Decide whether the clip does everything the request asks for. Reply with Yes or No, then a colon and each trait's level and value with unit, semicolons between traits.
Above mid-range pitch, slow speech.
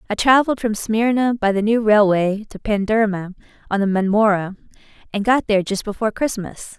No: high, 210 Hz; average, 170 wpm